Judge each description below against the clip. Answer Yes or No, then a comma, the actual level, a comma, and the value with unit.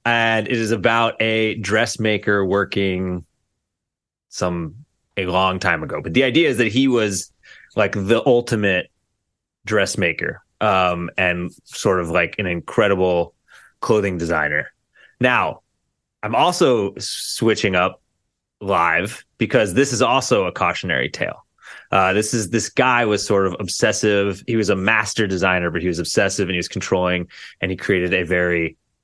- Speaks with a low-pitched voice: Yes, low, 100 Hz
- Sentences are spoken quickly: No, average, 150 wpm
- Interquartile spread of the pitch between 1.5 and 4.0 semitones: Yes, average, 3.4 semitones